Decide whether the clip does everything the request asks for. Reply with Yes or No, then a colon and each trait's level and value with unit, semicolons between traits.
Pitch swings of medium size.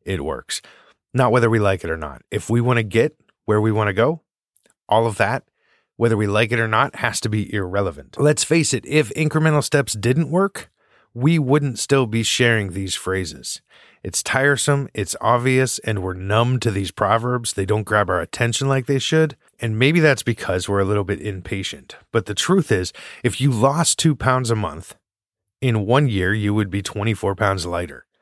Yes: average, 4.7 semitones